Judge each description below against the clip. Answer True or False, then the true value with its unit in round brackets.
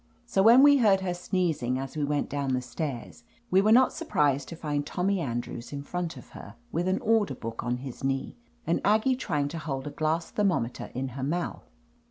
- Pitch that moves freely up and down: True (6.0 semitones)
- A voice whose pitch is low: False (155 Hz)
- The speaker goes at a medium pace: False (220 wpm)